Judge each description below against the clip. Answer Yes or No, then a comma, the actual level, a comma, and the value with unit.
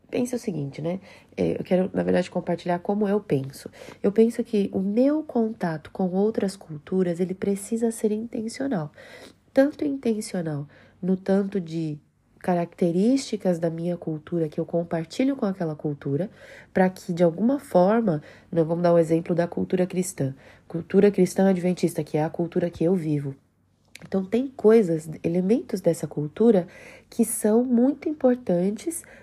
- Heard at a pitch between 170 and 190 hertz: Yes, medium, 185 Hz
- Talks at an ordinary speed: Yes, average, 150 wpm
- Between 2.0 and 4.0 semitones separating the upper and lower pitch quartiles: No, average, 4.7 semitones